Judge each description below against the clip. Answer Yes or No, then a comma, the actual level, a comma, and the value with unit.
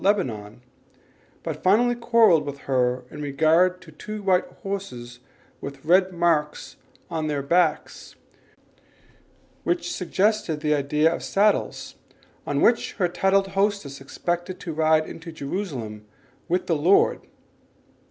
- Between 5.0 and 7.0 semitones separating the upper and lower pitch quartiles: Yes, wide, 5.4 semitones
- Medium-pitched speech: Yes, medium, 165 Hz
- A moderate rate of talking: No, slow, 125 wpm